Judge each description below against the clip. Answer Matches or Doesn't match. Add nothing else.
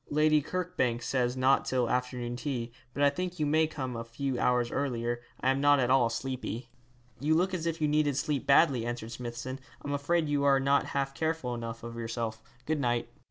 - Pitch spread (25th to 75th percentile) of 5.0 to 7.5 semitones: Doesn't match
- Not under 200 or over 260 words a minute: Matches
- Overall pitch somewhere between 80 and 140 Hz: Matches